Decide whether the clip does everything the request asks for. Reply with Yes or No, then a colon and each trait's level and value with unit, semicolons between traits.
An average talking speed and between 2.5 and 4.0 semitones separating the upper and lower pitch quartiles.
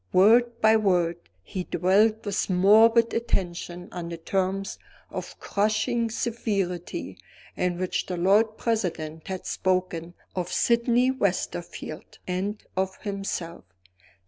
No: slow, 115 wpm; average, 3.7 semitones